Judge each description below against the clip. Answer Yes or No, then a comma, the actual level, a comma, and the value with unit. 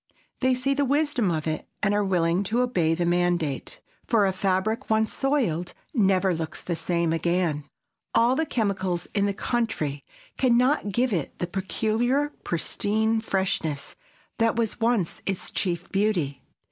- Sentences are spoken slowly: No, average, 155 wpm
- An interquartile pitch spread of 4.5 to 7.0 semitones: Yes, average, 5.2 semitones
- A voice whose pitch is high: Yes, high, 195 Hz